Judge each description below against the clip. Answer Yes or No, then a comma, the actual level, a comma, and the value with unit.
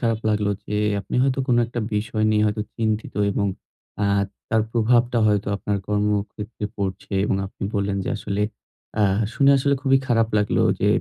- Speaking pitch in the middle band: No, low, 105 Hz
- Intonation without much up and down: Yes, narrow, 2.3 semitones